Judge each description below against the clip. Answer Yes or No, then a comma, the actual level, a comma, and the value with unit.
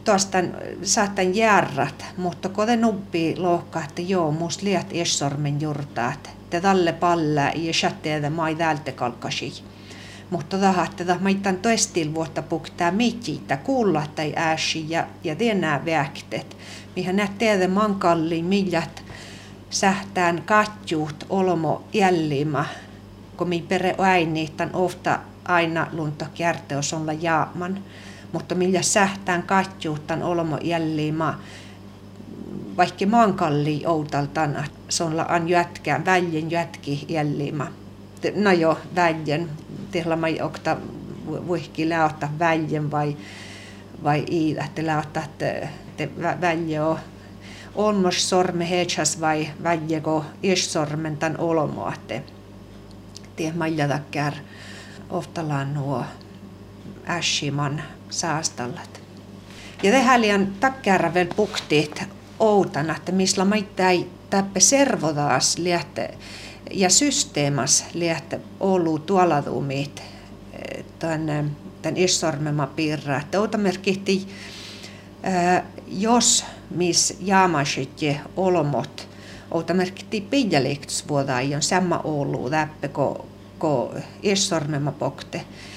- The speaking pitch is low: No, medium, 160 Hz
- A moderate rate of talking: No, slow, 95 wpm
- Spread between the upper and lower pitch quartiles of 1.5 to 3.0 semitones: No, average, 4.2 semitones